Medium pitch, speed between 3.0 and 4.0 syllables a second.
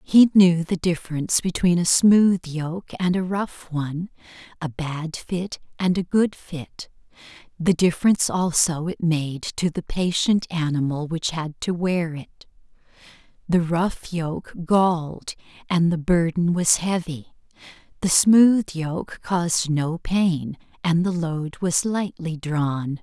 Yes: medium, 170 Hz; 3.8 syllables/s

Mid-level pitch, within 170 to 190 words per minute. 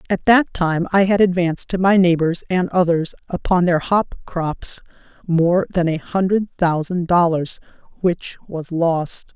No: medium, 175 Hz; average, 155 wpm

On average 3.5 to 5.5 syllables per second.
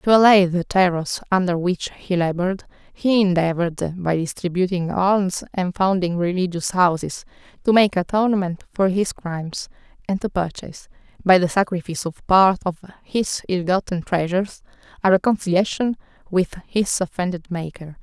Yes: 5.0 syllables/s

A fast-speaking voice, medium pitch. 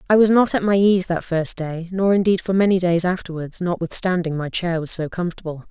Yes: fast, 220 wpm; medium, 175 Hz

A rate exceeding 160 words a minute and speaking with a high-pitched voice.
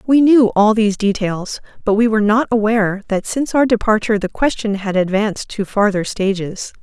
Yes: average, 185 wpm; high, 215 Hz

